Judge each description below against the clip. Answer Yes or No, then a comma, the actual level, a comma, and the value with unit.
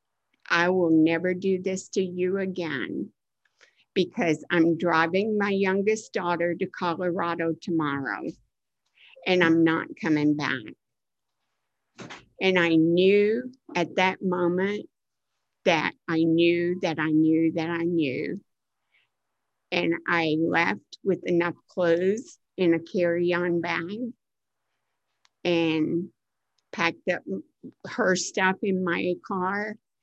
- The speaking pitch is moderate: Yes, medium, 175 Hz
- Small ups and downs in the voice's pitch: Yes, narrow, 2.3 semitones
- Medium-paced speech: No, slow, 110 wpm